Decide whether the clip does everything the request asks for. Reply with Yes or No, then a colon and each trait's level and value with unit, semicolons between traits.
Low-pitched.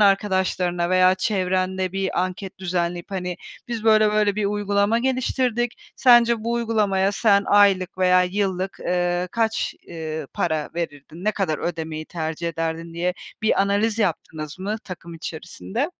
No: high, 190 Hz